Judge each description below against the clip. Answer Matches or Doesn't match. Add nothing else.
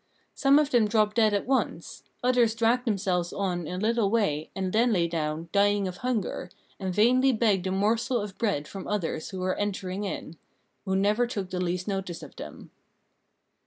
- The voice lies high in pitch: Matches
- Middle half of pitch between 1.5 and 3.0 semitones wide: Doesn't match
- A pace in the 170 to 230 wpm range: Matches